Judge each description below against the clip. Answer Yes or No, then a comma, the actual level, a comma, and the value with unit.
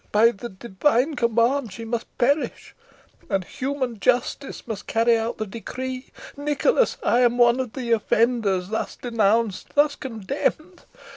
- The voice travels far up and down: No, average, 2.7 semitones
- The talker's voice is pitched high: Yes, high, 235 Hz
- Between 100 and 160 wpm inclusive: Yes, average, 140 wpm